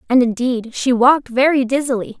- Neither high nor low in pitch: No, very high, 250 Hz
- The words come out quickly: No, average, 165 wpm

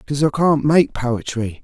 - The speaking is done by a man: Yes, male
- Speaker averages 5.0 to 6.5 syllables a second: Yes, 5.6 syllables/s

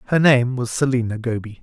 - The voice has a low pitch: Yes, low, 125 Hz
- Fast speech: No, average, 185 wpm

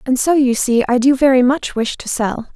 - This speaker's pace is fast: Yes, fast, 260 wpm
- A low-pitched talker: No, very high, 255 Hz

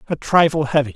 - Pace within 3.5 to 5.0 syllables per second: No, 6.5 syllables/s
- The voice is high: No, medium, 150 Hz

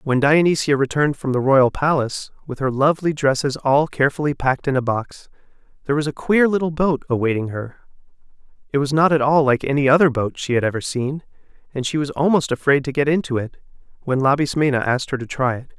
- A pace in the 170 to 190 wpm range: No, fast, 205 wpm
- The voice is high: No, medium, 140 Hz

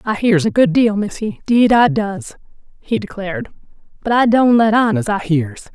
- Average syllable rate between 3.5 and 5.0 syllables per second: Yes, 4.7 syllables/s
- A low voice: No, high, 210 Hz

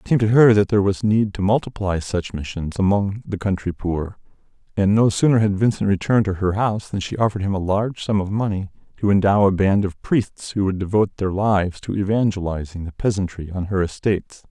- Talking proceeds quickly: Yes, fast, 215 wpm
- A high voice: No, low, 100 Hz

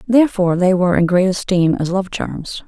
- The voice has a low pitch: No, medium, 185 Hz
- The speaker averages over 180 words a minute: Yes, average, 200 wpm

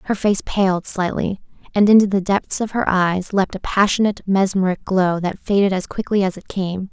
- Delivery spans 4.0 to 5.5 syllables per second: Yes, 5.1 syllables/s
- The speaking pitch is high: Yes, high, 195 Hz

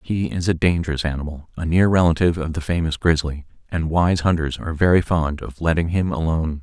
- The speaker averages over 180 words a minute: Yes, average, 200 wpm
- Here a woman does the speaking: No, male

